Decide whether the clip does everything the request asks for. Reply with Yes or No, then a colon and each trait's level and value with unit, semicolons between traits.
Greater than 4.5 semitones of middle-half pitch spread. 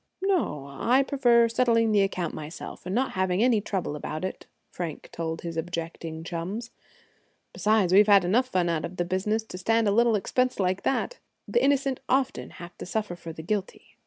Yes: average, 5.2 semitones